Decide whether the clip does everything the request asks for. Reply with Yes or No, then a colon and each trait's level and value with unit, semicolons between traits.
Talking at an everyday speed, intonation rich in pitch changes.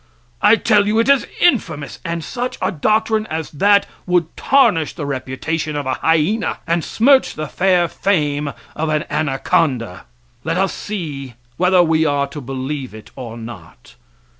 Yes: average, 160 wpm; wide, 6.1 semitones